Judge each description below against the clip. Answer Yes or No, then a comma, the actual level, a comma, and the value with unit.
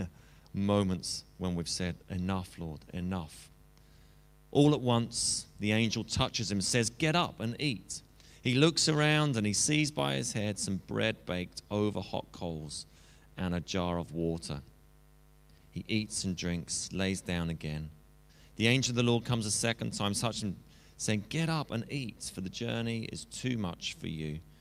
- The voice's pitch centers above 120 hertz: No, low, 100 Hz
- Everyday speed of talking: Yes, average, 170 wpm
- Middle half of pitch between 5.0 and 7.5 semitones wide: Yes, average, 5.3 semitones